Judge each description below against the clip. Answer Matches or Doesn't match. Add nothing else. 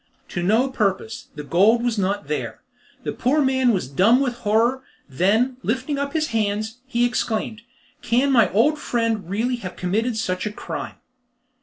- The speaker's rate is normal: Matches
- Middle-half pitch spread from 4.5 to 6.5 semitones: Doesn't match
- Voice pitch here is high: Matches